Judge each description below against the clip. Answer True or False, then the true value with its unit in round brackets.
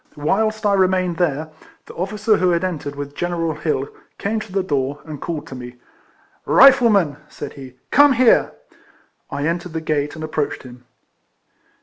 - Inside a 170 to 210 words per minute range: True (175 wpm)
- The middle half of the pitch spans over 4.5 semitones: True (5.3 semitones)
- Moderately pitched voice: True (165 Hz)